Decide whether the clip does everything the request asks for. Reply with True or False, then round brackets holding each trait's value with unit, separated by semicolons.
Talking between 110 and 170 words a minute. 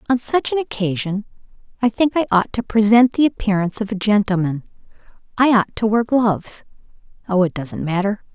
True (165 wpm)